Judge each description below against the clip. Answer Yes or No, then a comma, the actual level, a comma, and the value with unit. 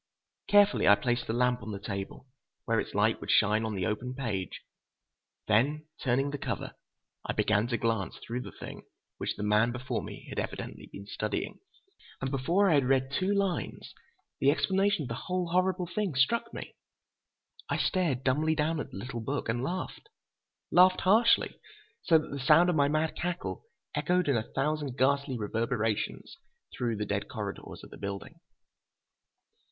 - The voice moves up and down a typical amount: No, wide, 6.9 semitones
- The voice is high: No, low, 135 Hz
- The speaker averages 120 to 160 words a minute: No, average, 175 wpm